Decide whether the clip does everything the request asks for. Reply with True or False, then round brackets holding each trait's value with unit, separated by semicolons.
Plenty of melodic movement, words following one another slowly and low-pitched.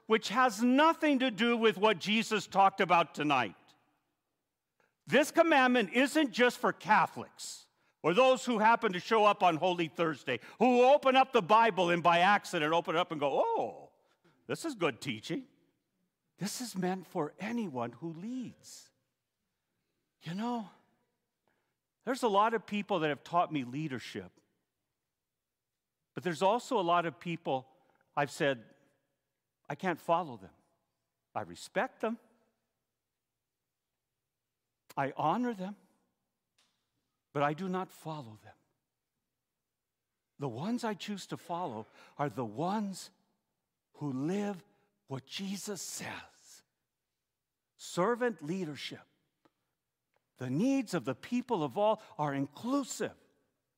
False (7.7 semitones; 125 wpm; 185 Hz)